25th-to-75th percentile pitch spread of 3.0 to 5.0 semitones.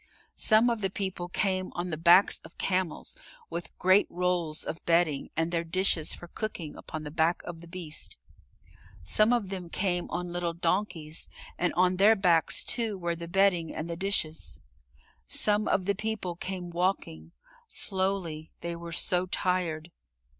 No: narrow, 2.4 semitones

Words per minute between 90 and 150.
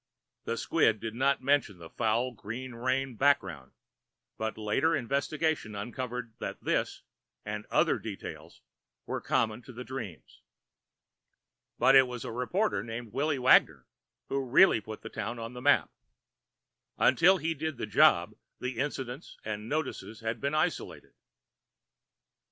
Yes: average, 140 wpm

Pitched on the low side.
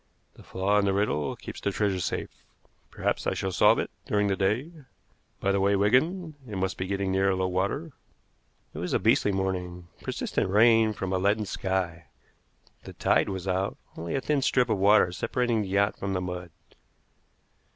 Yes: low, 100 Hz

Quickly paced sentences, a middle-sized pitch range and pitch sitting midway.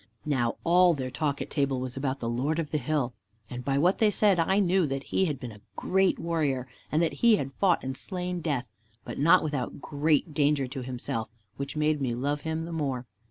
Yes: fast, 220 wpm; average, 4.1 semitones; medium, 145 Hz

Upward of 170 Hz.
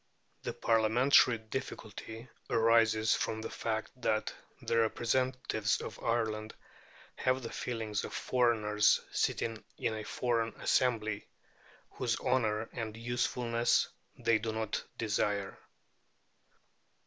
No: low, 115 Hz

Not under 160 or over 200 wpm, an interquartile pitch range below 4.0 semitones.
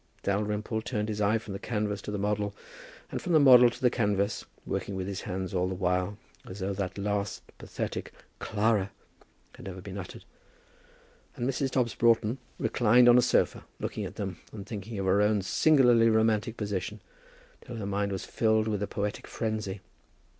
Yes: average, 180 wpm; narrow, 2.4 semitones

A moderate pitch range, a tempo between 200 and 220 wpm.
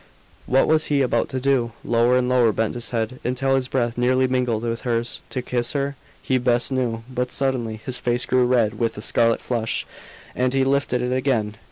No: narrow, 1.8 semitones; fast, 205 wpm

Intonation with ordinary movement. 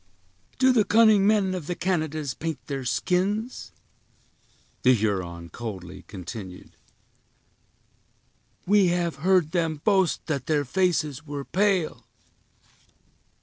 No: wide, 7.1 semitones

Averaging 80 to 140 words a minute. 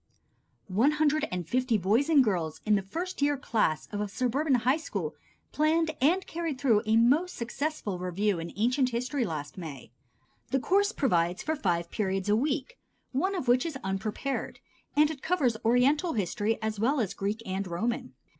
No: average, 175 wpm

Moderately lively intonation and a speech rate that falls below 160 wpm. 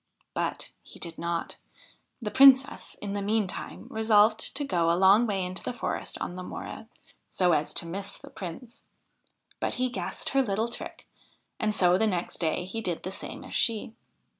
No: average, 3.9 semitones; average, 185 wpm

